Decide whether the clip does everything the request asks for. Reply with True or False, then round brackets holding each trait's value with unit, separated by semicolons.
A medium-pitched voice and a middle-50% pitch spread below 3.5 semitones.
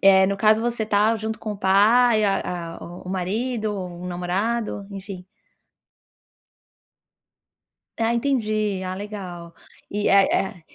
False (205 Hz; 2.8 semitones)